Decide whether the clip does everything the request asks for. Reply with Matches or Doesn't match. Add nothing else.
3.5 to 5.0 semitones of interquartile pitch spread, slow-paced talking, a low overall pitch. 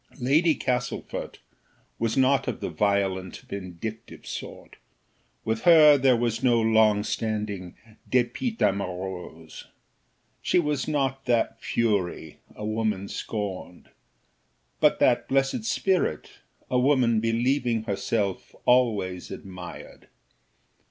Matches